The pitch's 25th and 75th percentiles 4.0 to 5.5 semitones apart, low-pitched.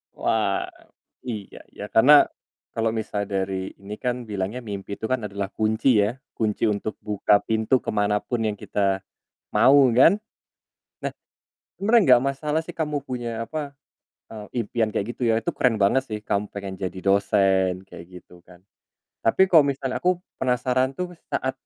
Yes: average, 4.3 semitones; low, 110 Hz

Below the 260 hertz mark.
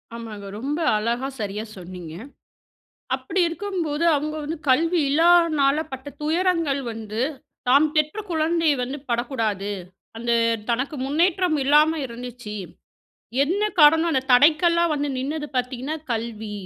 No: very high, 285 Hz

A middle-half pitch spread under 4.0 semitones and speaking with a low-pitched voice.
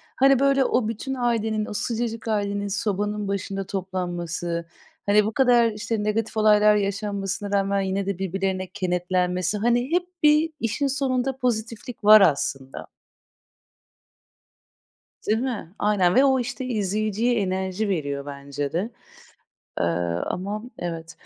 No: average, 3.6 semitones; high, 205 Hz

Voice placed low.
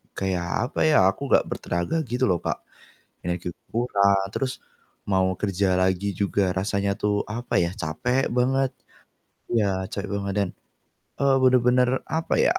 Yes: low, 100 Hz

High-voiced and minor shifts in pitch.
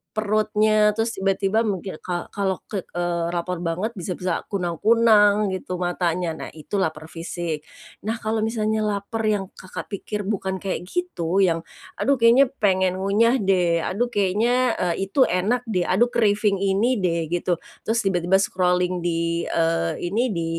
No: high, 195 Hz; average, 3.5 semitones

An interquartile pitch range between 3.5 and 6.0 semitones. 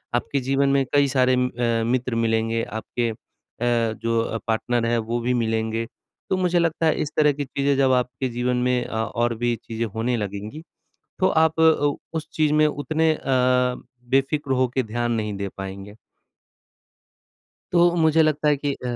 Yes: average, 4.2 semitones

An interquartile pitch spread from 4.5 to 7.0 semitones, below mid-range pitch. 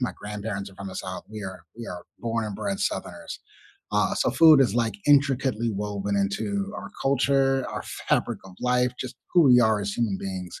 Yes: average, 5.1 semitones; low, 115 Hz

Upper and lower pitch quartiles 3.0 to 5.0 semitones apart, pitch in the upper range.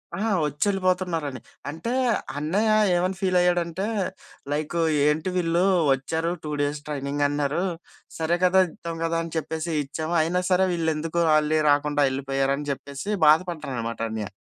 No: average, 3.3 semitones; medium, 160 Hz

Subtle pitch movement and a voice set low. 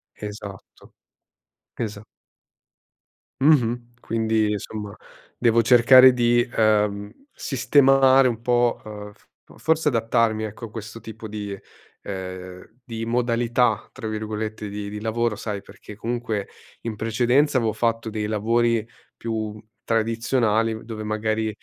Yes: narrow, 2.0 semitones; low, 110 Hz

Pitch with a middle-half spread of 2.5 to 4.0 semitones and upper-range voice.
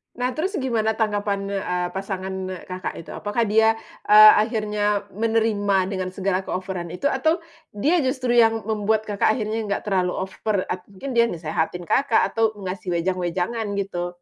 Yes: average, 3.1 semitones; high, 205 Hz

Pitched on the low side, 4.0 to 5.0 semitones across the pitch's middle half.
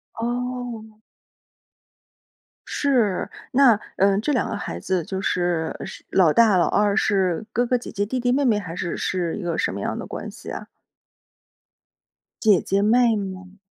No: high, 205 Hz; average, 4.4 semitones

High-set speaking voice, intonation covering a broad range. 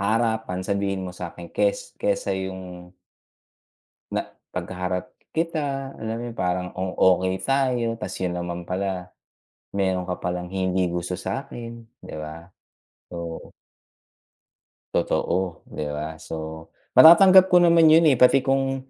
No: very low, 95 Hz; wide, 6.1 semitones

